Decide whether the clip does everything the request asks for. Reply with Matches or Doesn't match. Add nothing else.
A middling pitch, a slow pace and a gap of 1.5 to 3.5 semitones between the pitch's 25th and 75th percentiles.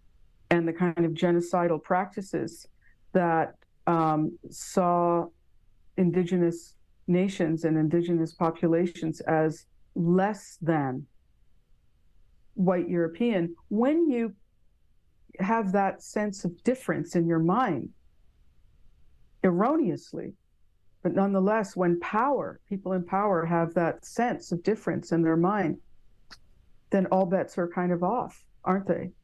Matches